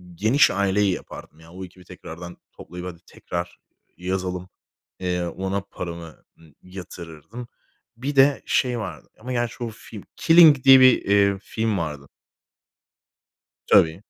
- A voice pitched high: No, very low, 95 Hz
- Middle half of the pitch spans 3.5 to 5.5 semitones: Yes, average, 4.6 semitones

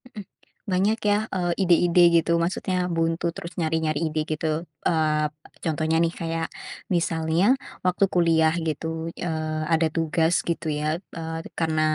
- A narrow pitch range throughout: Yes, narrow, 1.6 semitones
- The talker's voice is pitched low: No, medium, 165 Hz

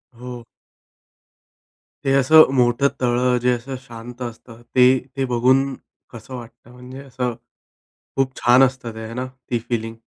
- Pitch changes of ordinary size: No, narrow, 1.5 semitones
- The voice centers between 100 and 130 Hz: Yes, low, 125 Hz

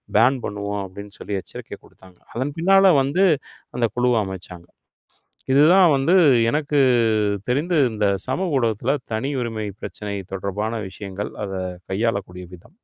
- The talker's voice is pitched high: No, low, 115 Hz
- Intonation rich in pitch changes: Yes, wide, 5.9 semitones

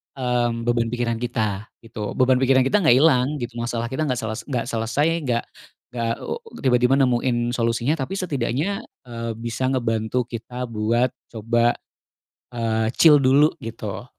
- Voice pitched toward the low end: Yes, low, 120 Hz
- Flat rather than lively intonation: Yes, narrow, 2.2 semitones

